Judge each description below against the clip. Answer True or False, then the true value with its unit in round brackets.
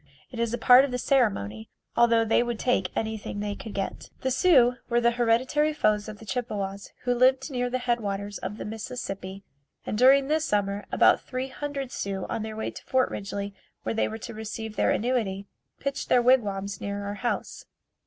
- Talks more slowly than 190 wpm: False (200 wpm)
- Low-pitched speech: False (225 Hz)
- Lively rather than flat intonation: False (3.7 semitones)